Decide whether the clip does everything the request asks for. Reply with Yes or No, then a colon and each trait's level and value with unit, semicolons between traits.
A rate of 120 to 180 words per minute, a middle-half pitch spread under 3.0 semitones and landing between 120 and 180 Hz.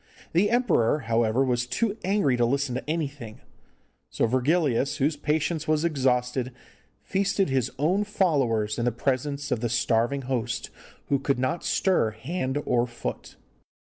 No: average, 150 wpm; average, 4.4 semitones; low, 135 Hz